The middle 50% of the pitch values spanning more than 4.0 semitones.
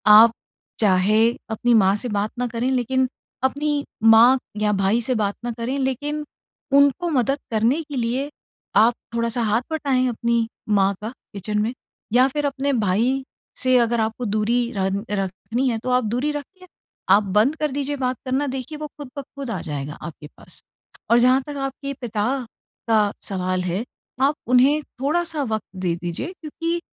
Yes: average, 4.7 semitones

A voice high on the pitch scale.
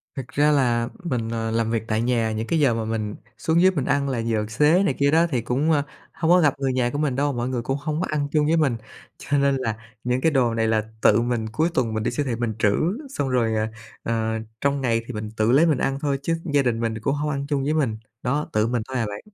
No: low, 130 Hz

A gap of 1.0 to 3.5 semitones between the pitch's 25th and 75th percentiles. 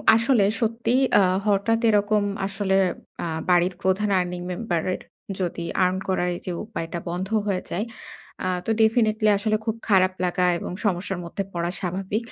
Yes: average, 3.2 semitones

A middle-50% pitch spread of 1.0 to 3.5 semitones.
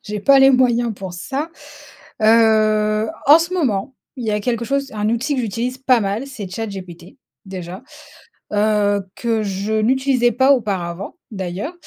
No: average, 4.2 semitones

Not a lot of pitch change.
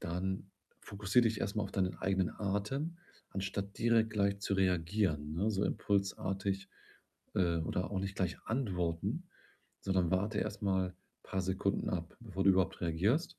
Yes: narrow, 1.9 semitones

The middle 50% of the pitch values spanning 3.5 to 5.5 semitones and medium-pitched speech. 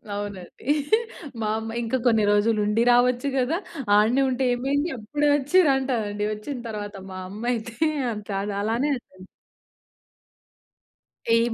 No: average, 3.8 semitones; high, 230 Hz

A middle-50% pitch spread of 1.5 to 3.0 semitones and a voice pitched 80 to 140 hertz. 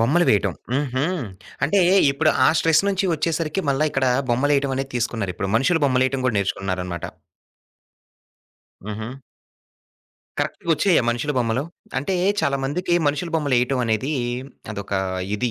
No: average, 5.0 semitones; low, 135 Hz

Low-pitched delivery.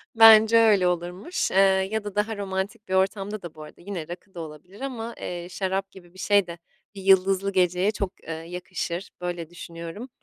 No: high, 190 Hz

